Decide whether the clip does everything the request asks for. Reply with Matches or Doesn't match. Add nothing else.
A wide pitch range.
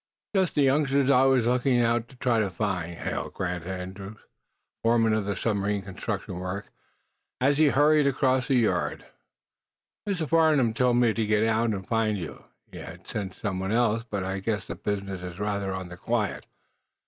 Doesn't match